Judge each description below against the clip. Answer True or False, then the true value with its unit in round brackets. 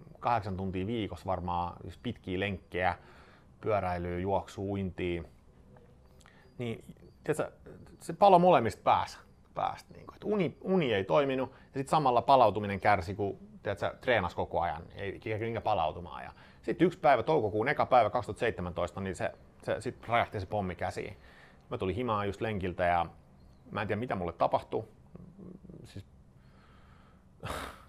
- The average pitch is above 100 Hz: False (95 Hz)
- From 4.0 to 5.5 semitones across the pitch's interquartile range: True (4.6 semitones)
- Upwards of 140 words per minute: False (130 wpm)